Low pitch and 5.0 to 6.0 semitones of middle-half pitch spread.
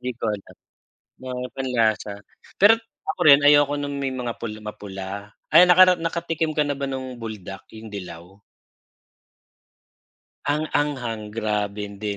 Yes: low, 125 Hz; wide, 5.5 semitones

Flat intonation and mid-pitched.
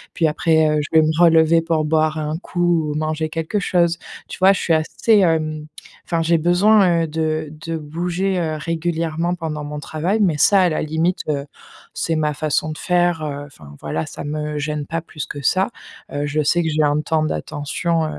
Yes: narrow, 2.0 semitones; medium, 160 Hz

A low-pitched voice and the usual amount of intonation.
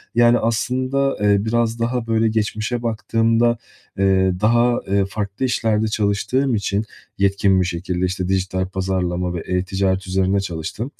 Yes: low, 100 Hz; average, 3.5 semitones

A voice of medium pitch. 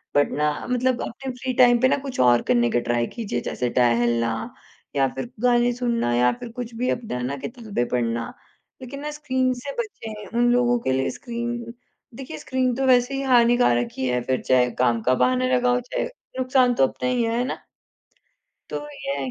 No: high, 235 Hz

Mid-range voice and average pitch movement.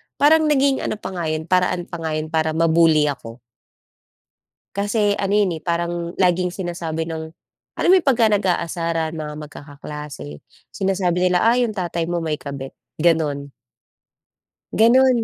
Yes: medium, 170 Hz; average, 4.0 semitones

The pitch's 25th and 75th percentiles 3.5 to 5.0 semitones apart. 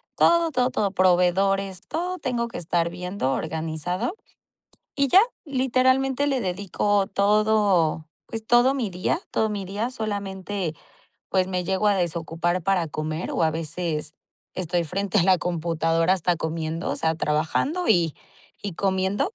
Yes: average, 4.4 semitones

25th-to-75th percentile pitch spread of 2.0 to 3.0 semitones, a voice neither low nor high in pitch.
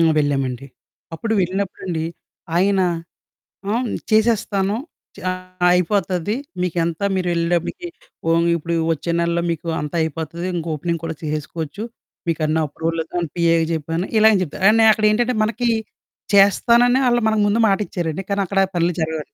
No: average, 3.8 semitones; medium, 175 Hz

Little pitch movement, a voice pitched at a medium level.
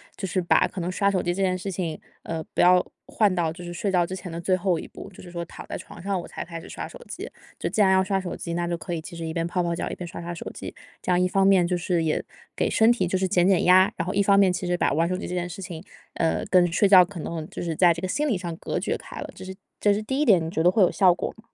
Yes: narrow, 2.0 semitones; medium, 180 Hz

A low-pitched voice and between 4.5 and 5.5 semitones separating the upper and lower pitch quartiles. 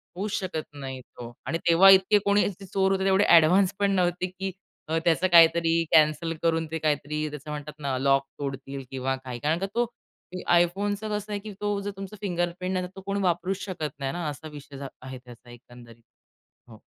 No: medium, 170 Hz; average, 5.1 semitones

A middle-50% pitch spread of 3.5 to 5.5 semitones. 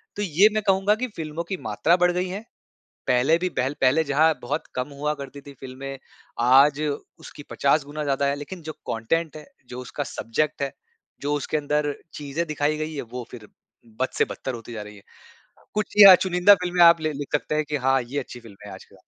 Yes: average, 3.9 semitones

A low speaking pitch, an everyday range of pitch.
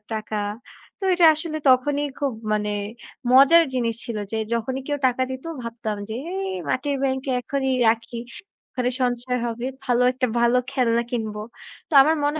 No: very high, 250 Hz; average, 3.1 semitones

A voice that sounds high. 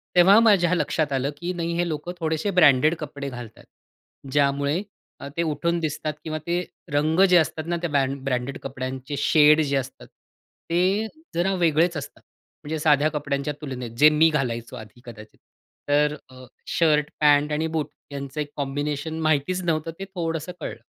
No: medium, 150 Hz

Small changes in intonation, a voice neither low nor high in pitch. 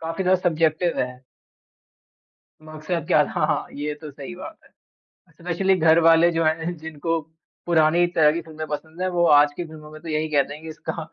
Yes: narrow, 1.8 semitones; medium, 160 Hz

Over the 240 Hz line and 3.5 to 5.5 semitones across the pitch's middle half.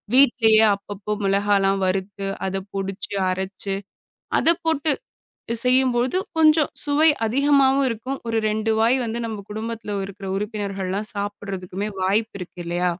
No: high, 210 Hz; average, 4.2 semitones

